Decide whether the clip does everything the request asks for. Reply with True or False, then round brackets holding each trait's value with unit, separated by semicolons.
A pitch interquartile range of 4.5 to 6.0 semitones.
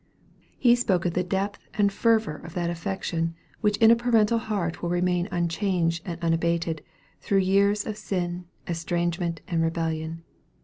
False (3.3 semitones)